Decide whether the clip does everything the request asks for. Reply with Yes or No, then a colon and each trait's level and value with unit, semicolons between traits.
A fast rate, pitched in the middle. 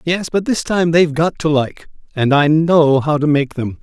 Yes: fast, 235 wpm; medium, 155 Hz